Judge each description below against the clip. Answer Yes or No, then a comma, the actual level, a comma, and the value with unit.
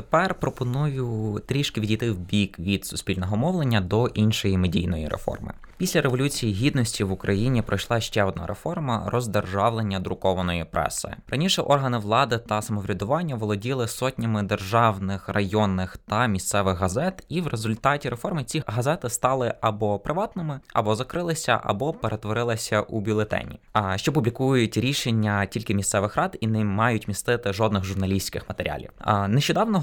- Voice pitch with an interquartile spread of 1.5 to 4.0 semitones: No, average, 4.4 semitones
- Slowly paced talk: No, average, 135 wpm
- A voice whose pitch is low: Yes, low, 110 Hz